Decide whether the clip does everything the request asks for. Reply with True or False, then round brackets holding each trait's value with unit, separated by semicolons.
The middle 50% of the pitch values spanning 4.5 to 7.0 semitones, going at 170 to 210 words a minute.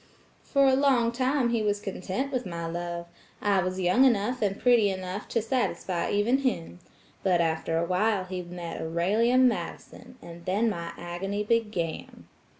False (5.2 semitones; 160 wpm)